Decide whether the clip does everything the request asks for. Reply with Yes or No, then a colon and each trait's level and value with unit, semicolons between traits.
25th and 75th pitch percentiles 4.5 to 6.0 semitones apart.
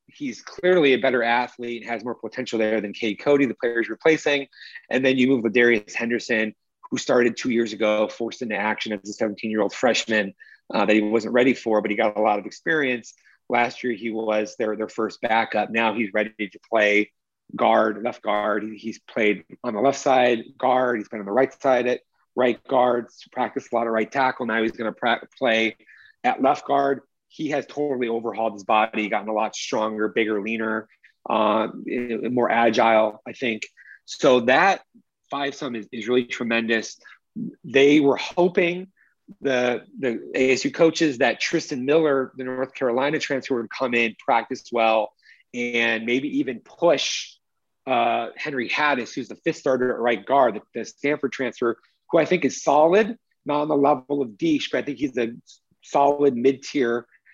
No: average, 3.6 semitones